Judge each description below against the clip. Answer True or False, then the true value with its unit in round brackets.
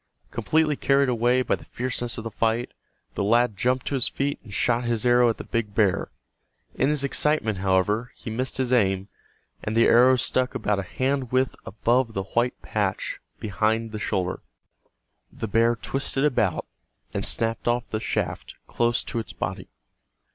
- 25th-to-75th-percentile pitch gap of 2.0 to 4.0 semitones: True (2.9 semitones)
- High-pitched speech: False (120 Hz)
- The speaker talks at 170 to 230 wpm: True (175 wpm)